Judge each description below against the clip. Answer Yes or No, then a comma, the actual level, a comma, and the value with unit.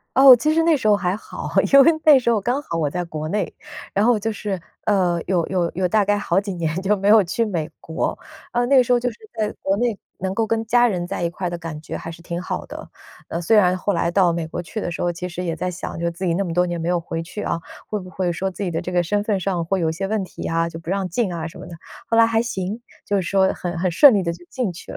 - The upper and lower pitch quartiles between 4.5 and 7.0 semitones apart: No, average, 3.8 semitones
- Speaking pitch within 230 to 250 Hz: No, medium, 185 Hz